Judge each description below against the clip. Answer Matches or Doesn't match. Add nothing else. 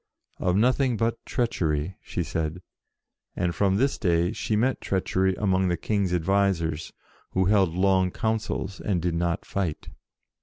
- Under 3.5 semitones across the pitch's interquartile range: Matches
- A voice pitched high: Doesn't match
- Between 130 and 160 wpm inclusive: Matches